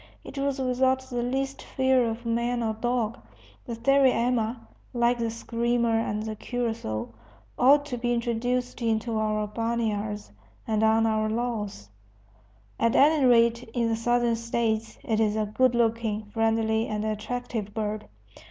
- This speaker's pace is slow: No, average, 145 wpm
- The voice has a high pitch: Yes, high, 230 Hz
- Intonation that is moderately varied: No, narrow, 1.9 semitones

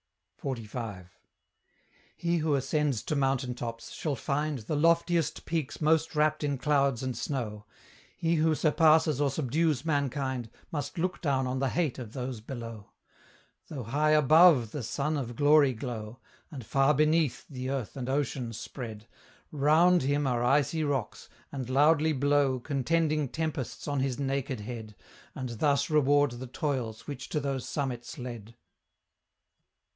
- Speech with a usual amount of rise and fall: Yes, average, 3.5 semitones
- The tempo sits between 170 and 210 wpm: No, average, 145 wpm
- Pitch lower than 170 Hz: Yes, medium, 140 Hz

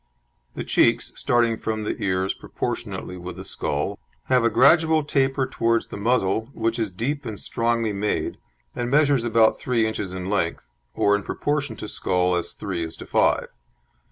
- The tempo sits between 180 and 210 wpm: No, average, 170 wpm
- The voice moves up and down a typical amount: Yes, average, 4.6 semitones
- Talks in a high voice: No, low, 110 Hz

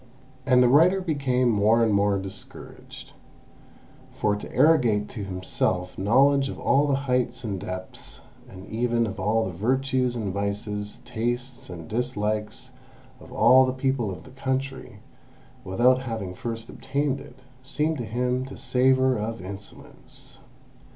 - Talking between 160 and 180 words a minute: No, average, 145 wpm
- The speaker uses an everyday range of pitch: Yes, average, 4.2 semitones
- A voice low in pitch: Yes, low, 120 Hz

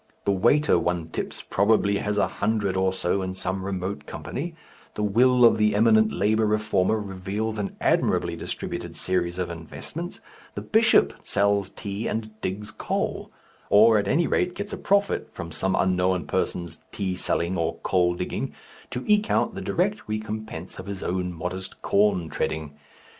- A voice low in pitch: Yes, low, 100 Hz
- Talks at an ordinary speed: Yes, average, 165 wpm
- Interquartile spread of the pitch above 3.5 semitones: No, average, 3.0 semitones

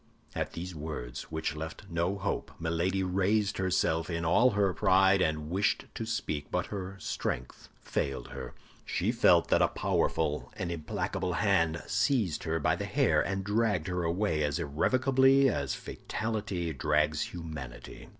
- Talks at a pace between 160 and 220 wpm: No, average, 150 wpm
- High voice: No, very low, 85 Hz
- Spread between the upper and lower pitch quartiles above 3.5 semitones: Yes, average, 4.1 semitones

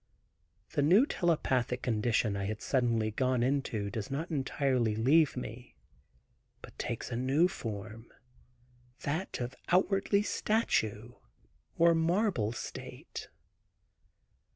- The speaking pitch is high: No, low, 130 Hz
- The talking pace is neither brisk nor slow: No, slow, 105 wpm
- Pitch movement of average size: No, wide, 6.5 semitones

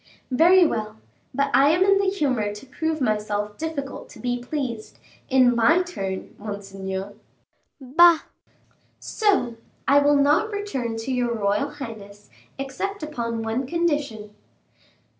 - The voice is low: No, very high, 260 Hz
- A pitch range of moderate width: No, wide, 6.3 semitones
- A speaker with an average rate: No, slow, 130 wpm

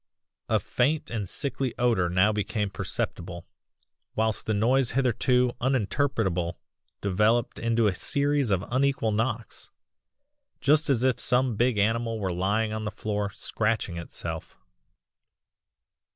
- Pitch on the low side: Yes, low, 115 Hz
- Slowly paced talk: Yes, slow, 125 wpm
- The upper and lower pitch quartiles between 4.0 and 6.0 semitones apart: No, average, 3.6 semitones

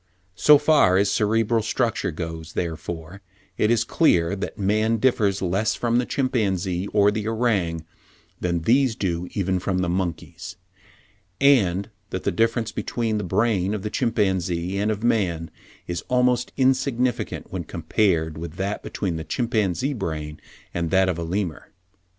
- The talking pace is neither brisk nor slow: Yes, average, 150 wpm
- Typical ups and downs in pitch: Yes, average, 4.6 semitones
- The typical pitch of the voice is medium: No, low, 100 Hz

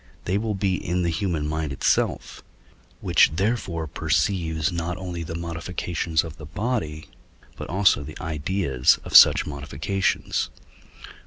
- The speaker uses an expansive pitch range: No, average, 3.3 semitones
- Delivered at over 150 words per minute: No, slow, 135 wpm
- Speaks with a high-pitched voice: No, very low, 85 Hz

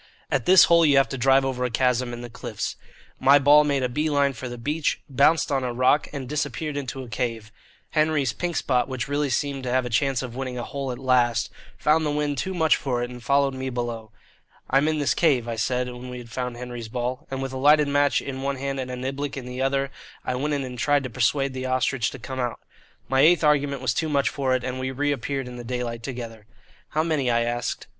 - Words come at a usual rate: No, fast, 245 wpm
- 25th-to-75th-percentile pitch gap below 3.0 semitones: Yes, narrow, 2.5 semitones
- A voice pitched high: No, low, 130 Hz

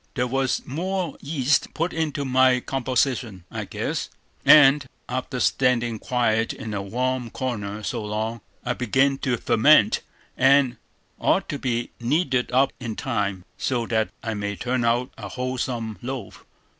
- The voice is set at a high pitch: No, low, 125 Hz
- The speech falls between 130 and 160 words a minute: Yes, average, 145 wpm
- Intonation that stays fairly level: No, average, 3.0 semitones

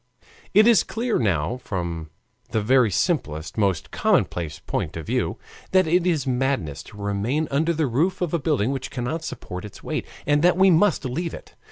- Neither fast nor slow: Yes, average, 185 wpm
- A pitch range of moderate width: No, wide, 8.7 semitones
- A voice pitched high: No, low, 135 Hz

